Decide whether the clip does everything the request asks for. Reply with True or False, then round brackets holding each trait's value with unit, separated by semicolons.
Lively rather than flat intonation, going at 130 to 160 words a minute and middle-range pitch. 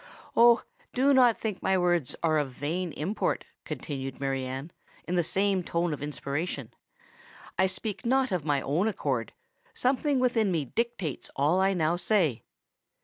True (6.7 semitones; 150 wpm; 175 Hz)